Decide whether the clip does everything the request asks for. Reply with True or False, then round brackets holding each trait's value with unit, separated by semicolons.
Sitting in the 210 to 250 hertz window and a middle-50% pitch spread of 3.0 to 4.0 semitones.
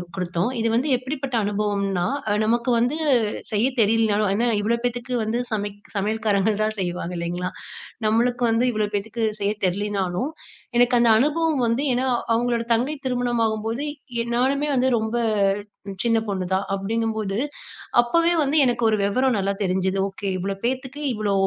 True (225 Hz; 3.5 semitones)